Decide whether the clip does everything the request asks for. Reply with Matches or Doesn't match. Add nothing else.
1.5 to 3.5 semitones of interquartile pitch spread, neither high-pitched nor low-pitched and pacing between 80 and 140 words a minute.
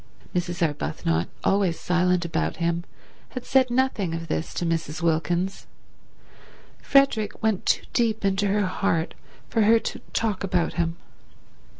Doesn't match